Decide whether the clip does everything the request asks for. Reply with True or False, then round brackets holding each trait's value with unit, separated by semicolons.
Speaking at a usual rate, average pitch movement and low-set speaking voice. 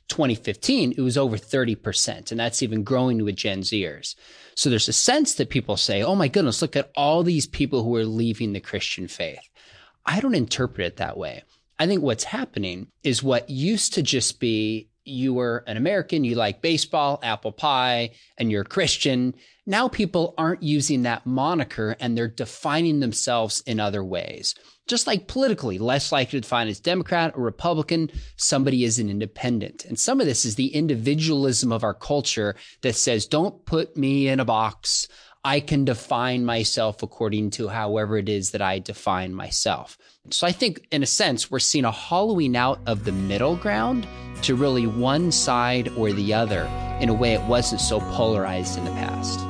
True (185 wpm; 4.6 semitones; 120 Hz)